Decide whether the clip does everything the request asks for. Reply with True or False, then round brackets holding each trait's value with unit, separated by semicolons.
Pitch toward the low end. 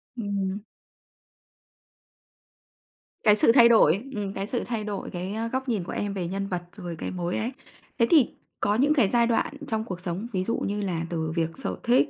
False (205 Hz)